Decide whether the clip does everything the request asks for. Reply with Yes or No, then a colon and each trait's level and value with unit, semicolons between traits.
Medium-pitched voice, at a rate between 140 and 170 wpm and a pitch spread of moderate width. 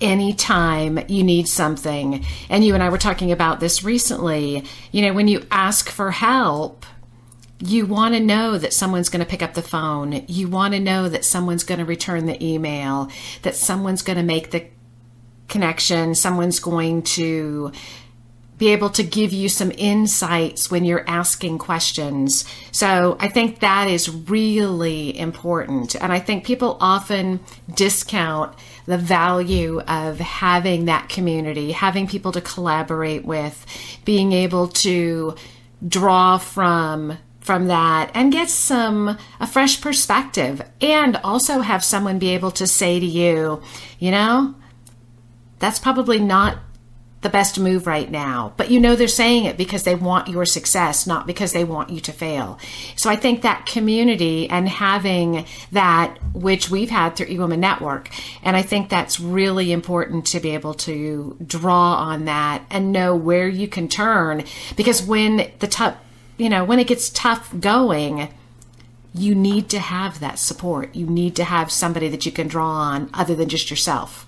Yes: medium, 175 Hz; average, 165 wpm; average, 4.2 semitones